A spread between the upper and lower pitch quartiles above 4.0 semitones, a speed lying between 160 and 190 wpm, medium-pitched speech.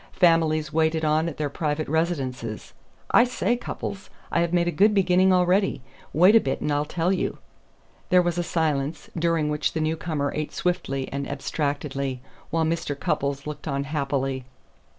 No: average, 3.5 semitones; average, 170 wpm; medium, 155 Hz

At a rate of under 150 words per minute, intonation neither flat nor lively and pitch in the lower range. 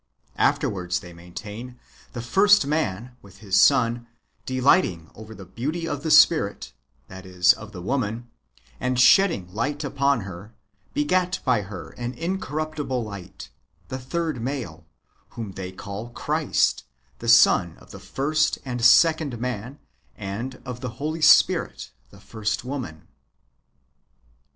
No: average, 140 wpm; wide, 6.3 semitones; low, 120 Hz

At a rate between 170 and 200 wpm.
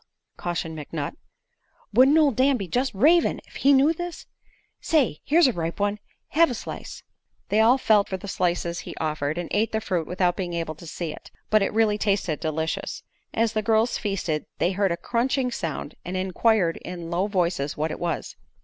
Yes: average, 195 wpm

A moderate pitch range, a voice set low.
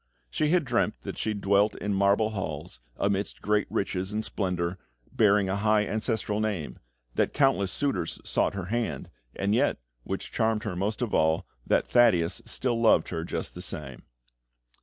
Yes: average, 3.1 semitones; low, 100 Hz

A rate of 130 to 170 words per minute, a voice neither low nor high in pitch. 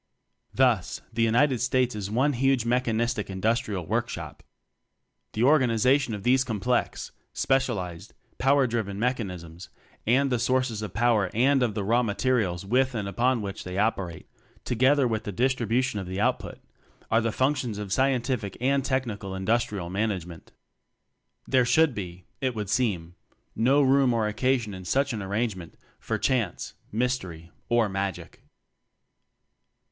No: average, 150 wpm; low, 115 Hz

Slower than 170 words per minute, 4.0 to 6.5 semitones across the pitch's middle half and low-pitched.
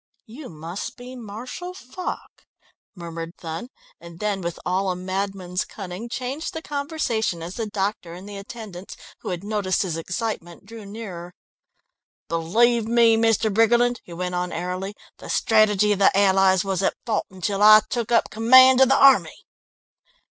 No: average, 160 wpm; average, 4.3 semitones; high, 205 Hz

